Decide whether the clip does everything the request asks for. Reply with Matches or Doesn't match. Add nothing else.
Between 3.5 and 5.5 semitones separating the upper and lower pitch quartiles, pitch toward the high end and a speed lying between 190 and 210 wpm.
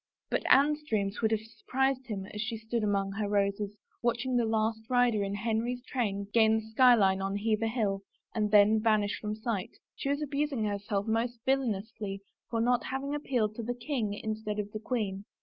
Doesn't match